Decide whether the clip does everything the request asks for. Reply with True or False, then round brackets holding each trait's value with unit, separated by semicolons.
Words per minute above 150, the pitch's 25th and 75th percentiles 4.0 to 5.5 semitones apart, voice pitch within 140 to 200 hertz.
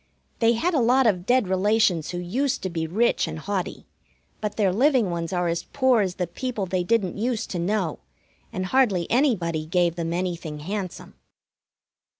True (175 wpm; 5.0 semitones; 190 Hz)